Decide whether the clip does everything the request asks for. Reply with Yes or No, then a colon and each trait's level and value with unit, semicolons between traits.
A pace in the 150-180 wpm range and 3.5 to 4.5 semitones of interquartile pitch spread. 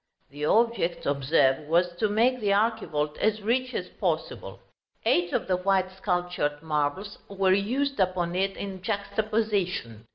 No: average, 140 wpm; average, 4.1 semitones